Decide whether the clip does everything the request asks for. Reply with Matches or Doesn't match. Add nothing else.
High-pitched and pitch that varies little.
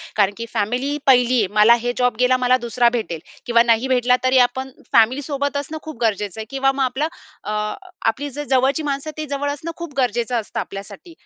Doesn't match